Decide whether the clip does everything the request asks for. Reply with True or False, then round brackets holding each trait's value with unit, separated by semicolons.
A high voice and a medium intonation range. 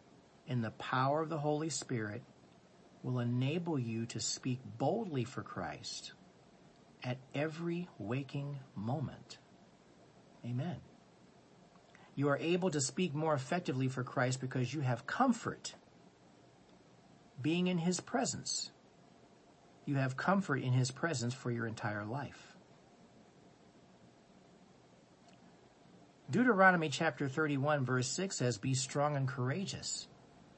False (135 Hz; 4.1 semitones)